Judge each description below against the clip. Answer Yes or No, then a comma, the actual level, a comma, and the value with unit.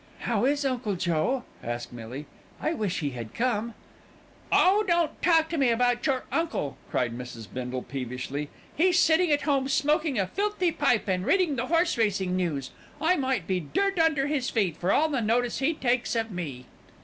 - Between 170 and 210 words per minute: Yes, average, 185 wpm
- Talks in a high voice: Yes, high, 240 Hz